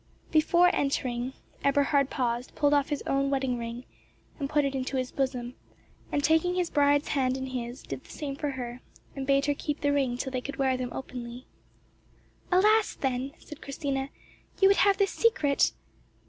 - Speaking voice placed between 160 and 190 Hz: No, very high, 275 Hz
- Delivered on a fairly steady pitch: Yes, narrow, 2.3 semitones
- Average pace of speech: Yes, average, 180 wpm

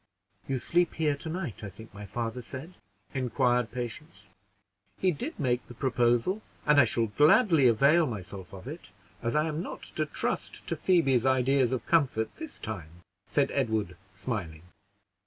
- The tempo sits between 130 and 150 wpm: No, average, 160 wpm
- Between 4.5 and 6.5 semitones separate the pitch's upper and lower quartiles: Yes, average, 5.3 semitones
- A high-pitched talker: No, low, 125 Hz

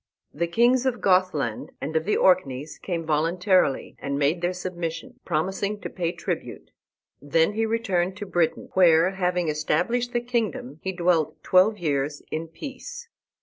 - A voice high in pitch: No, medium, 180 Hz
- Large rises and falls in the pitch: No, average, 4.1 semitones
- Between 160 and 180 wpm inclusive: No, average, 150 wpm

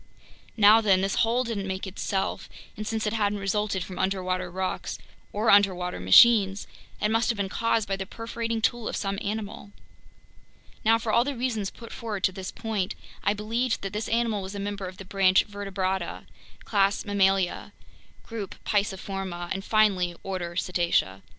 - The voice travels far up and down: No, narrow, 2.6 semitones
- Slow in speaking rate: No, average, 170 wpm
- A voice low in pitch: No, high, 200 Hz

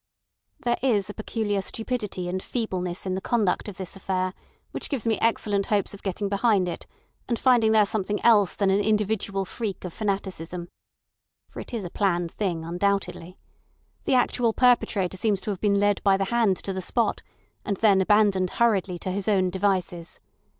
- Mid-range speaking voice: No, high, 200 Hz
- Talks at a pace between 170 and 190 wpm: Yes, average, 180 wpm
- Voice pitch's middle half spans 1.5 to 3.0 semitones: Yes, average, 2.7 semitones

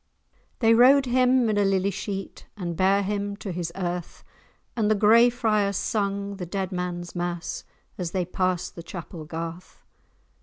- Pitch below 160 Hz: No, high, 195 Hz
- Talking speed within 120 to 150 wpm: No, average, 160 wpm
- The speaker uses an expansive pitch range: No, average, 3.1 semitones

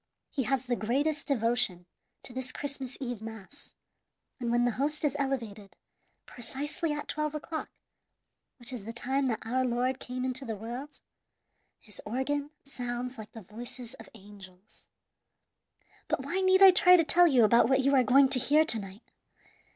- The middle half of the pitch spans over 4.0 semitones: No, average, 3.6 semitones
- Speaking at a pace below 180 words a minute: Yes, average, 170 wpm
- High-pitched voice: Yes, very high, 255 Hz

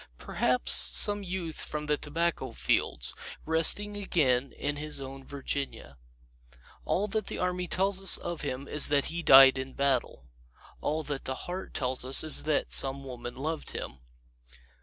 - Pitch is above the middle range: No, medium, 150 Hz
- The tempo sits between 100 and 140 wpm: No, average, 155 wpm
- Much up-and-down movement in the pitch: No, average, 4.3 semitones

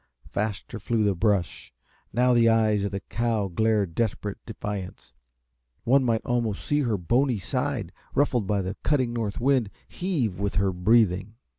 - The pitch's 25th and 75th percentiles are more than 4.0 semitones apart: No, average, 3.3 semitones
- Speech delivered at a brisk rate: No, average, 155 wpm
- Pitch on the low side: Yes, low, 110 Hz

